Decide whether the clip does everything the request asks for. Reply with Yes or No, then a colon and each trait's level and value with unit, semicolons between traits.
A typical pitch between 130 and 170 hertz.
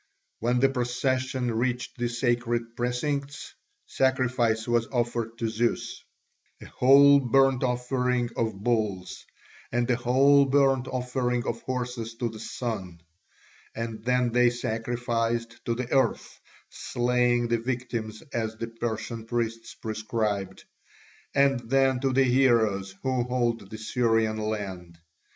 No: low, 120 Hz